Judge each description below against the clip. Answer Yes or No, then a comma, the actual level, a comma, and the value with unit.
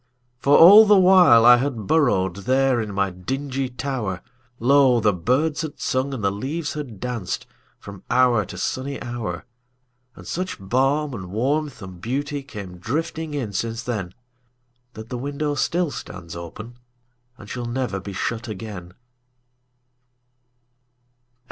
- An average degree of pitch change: Yes, average, 4.9 semitones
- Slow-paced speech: Yes, slow, 125 wpm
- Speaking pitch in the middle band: No, low, 125 Hz